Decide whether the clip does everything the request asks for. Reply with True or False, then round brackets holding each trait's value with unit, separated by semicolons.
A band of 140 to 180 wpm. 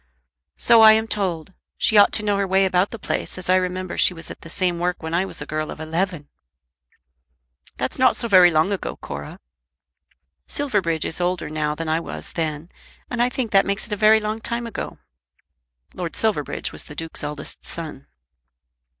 False (195 wpm)